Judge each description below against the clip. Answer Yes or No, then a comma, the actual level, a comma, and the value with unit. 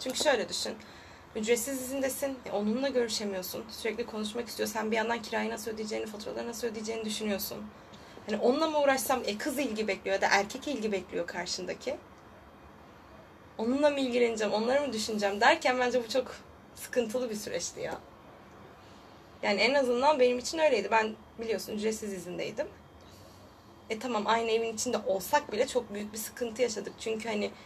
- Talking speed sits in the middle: No, fast, 160 wpm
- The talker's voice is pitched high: Yes, high, 225 Hz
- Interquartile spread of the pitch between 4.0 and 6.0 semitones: No, average, 3.0 semitones